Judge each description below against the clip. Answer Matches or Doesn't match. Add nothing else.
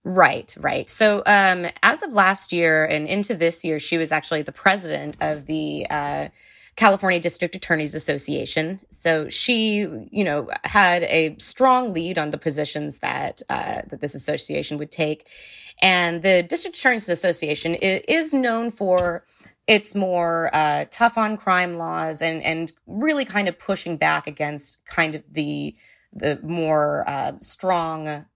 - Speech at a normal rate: Matches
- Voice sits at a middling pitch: Matches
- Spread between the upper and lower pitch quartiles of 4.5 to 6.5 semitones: Doesn't match